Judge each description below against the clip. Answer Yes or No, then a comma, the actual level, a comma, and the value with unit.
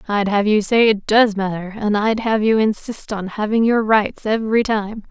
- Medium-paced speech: No, fast, 210 wpm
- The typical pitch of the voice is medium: No, high, 215 Hz